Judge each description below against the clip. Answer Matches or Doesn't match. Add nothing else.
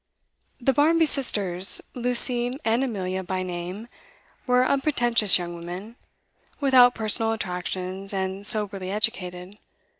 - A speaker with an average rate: Doesn't match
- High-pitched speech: Matches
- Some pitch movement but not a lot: Matches